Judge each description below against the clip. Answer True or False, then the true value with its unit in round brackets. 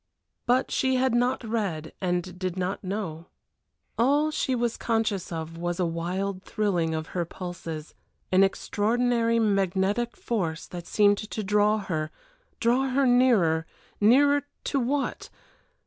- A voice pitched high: True (205 Hz)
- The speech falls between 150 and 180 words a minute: False (135 wpm)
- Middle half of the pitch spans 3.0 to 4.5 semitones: False (5.4 semitones)